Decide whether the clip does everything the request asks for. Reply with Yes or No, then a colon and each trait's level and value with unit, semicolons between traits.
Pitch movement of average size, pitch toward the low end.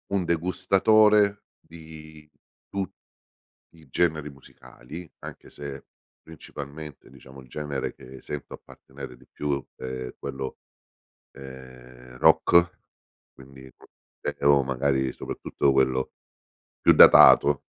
Yes: average, 3.5 semitones; very low, 70 Hz